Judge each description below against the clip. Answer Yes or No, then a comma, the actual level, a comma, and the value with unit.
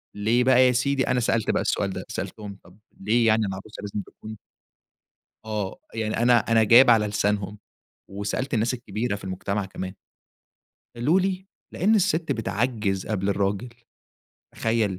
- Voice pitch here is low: Yes, low, 110 Hz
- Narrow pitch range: No, average, 3.4 semitones